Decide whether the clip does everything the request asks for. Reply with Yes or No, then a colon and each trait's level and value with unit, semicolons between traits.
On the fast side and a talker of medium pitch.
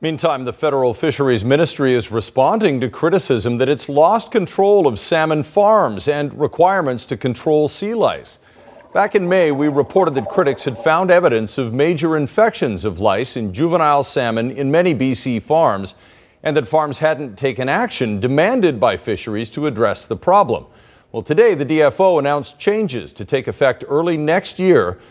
No: average, 165 wpm; medium, 150 Hz